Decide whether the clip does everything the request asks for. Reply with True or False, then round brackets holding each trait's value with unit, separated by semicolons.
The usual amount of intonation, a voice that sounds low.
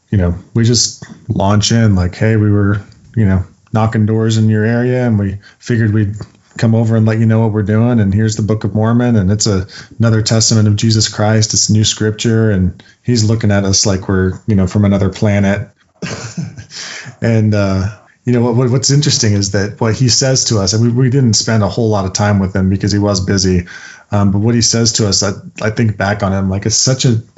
False (2.3 semitones; 110 Hz)